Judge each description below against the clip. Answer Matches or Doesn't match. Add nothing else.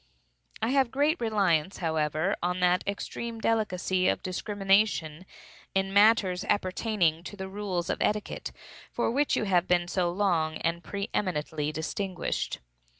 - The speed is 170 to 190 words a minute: Doesn't match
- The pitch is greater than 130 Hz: Matches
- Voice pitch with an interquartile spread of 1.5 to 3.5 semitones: Matches